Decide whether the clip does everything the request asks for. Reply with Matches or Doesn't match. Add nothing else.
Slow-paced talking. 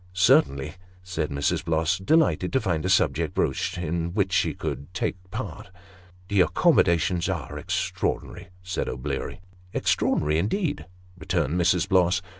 Doesn't match